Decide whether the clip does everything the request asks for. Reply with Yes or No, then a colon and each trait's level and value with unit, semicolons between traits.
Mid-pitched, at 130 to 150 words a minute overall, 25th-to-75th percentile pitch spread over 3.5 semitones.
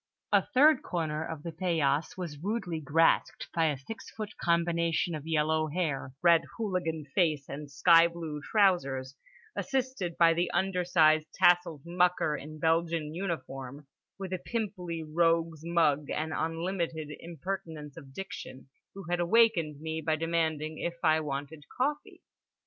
No: medium, 165 Hz; average, 140 wpm; narrow, 2.5 semitones